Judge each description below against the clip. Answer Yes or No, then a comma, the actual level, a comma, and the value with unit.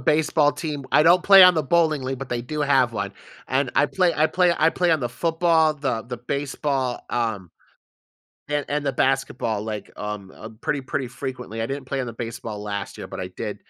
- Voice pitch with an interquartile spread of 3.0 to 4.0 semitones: No, average, 4.5 semitones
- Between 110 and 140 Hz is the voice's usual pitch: Yes, low, 135 Hz